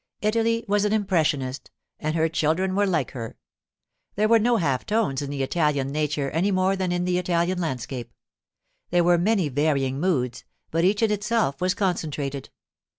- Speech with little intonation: No, wide, 5.6 semitones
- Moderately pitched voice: Yes, medium, 170 Hz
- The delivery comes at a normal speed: Yes, average, 170 wpm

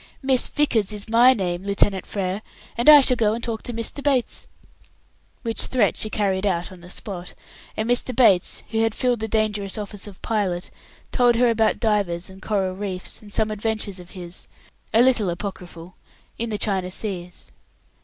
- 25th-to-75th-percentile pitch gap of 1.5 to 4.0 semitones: Yes, average, 3.4 semitones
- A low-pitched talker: No, high, 210 Hz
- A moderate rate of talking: Yes, average, 180 wpm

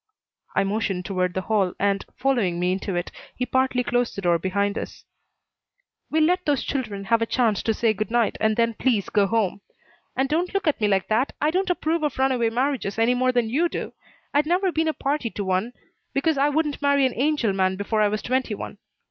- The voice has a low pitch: No, high, 235 Hz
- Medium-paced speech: No, fast, 220 wpm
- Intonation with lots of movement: Yes, wide, 5.8 semitones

